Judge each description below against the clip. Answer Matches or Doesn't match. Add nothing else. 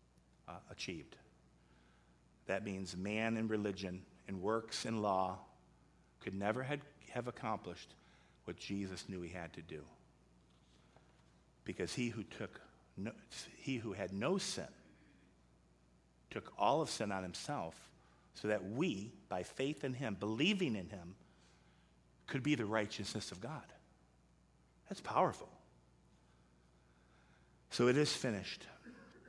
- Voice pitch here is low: Matches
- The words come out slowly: Matches